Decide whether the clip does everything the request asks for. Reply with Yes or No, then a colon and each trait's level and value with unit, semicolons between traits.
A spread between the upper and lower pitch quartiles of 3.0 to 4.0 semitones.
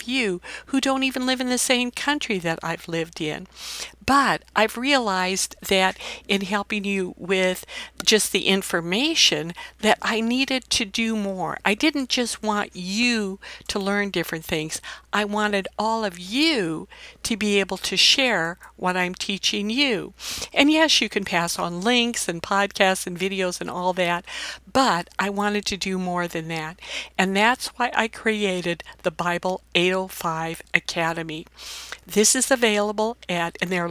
No: average, 4.6 semitones